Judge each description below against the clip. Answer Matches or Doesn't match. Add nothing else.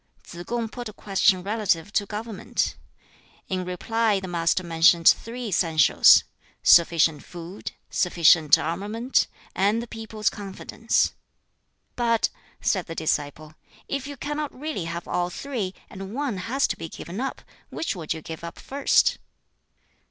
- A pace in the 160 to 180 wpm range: Doesn't match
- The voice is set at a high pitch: Matches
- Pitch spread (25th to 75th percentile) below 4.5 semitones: Doesn't match